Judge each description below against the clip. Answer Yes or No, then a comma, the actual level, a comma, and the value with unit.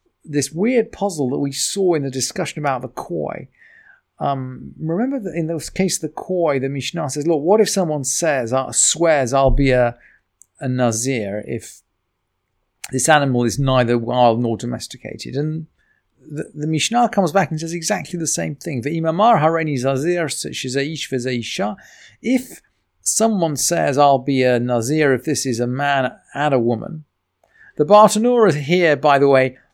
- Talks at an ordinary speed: Yes, average, 155 wpm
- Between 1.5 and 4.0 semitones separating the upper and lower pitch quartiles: No, average, 4.6 semitones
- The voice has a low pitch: No, medium, 145 Hz